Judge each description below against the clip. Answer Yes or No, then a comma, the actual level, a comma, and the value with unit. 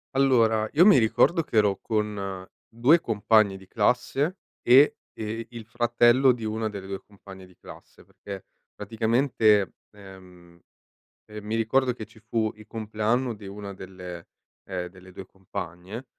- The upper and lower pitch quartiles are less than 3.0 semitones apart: No, average, 3.4 semitones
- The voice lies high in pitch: No, low, 110 Hz